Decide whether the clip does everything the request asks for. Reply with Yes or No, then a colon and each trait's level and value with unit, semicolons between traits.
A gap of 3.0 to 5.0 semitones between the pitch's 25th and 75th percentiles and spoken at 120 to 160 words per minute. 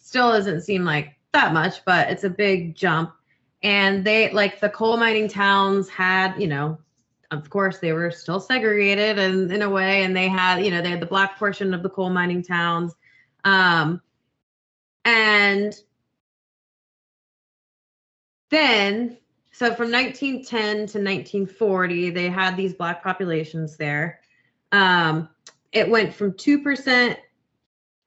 Yes: average, 3.4 semitones; average, 140 wpm